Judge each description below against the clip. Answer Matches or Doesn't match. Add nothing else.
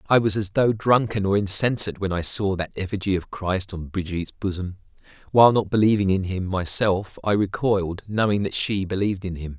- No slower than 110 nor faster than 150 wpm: Doesn't match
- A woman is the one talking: Doesn't match